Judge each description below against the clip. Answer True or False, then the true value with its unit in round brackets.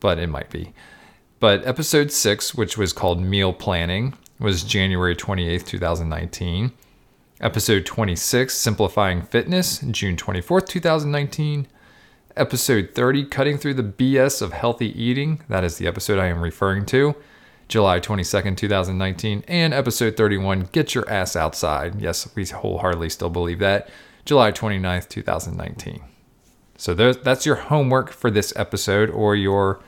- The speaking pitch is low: True (105 Hz)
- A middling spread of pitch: False (5.7 semitones)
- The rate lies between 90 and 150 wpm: True (135 wpm)